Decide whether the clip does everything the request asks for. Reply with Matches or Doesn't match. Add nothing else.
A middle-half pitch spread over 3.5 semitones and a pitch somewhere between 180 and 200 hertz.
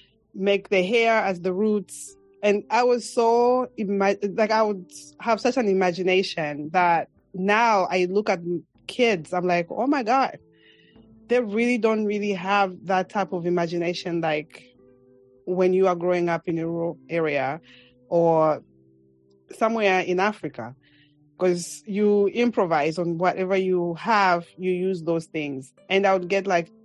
Matches